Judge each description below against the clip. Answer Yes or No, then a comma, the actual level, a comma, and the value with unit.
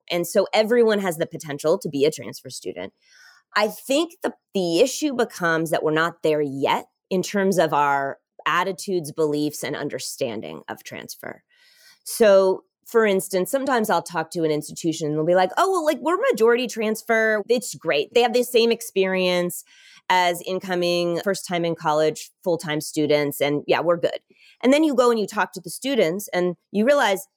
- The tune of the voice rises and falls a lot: Yes, wide, 6.1 semitones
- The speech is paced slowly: No, average, 185 wpm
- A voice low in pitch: No, high, 190 Hz